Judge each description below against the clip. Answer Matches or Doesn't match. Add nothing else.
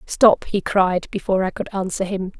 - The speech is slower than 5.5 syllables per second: Matches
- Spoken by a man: Doesn't match